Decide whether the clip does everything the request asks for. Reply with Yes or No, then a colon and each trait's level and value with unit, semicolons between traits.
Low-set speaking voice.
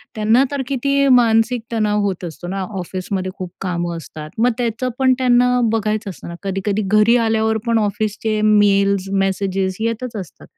No: high, 215 Hz